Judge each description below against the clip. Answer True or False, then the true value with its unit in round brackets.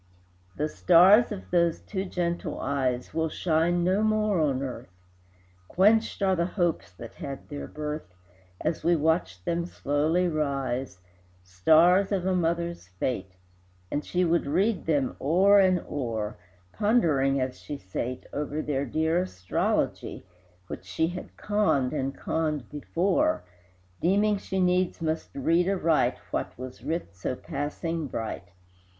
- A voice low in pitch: False (160 Hz)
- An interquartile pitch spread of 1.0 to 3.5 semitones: False (4.8 semitones)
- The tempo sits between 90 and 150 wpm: True (140 wpm)